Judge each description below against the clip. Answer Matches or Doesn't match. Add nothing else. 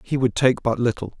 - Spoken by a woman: Doesn't match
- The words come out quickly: Matches